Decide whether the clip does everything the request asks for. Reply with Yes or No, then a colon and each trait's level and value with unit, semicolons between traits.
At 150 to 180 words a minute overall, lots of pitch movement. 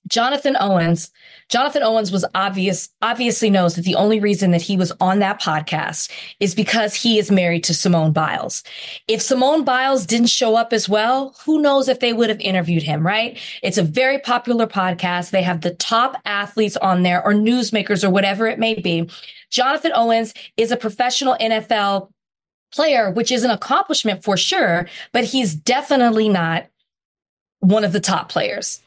No: average, 175 wpm; average, 4.3 semitones